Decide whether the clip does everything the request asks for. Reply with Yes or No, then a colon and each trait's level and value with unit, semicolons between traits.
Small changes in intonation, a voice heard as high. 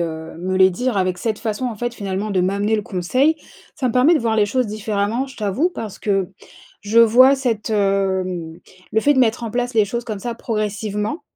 No: average, 3.6 semitones; high, 215 Hz